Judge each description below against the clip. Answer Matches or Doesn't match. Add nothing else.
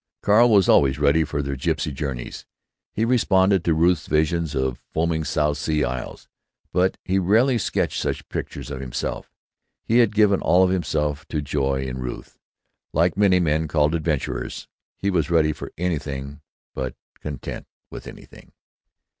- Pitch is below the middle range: Matches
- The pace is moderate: Matches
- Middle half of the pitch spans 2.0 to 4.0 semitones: Doesn't match